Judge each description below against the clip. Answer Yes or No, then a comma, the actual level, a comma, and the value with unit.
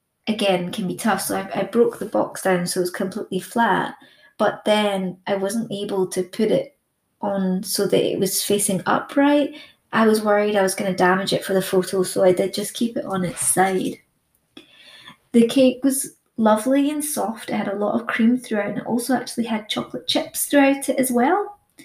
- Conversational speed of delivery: No, fast, 210 wpm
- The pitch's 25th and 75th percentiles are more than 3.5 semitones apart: Yes, average, 4.4 semitones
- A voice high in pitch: Yes, high, 205 Hz